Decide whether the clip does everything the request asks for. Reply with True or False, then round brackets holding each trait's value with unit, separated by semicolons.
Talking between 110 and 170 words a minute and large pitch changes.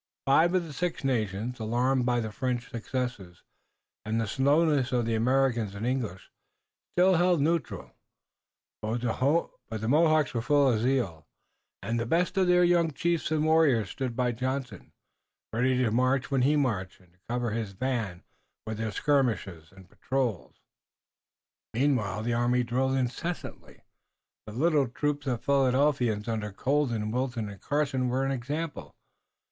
False (150 wpm; 4.1 semitones)